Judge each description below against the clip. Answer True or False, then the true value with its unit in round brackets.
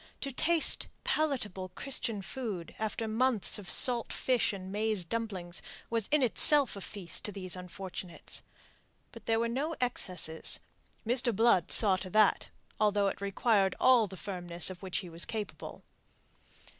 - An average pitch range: True (4.2 semitones)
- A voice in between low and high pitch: False (210 Hz)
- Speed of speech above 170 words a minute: False (150 wpm)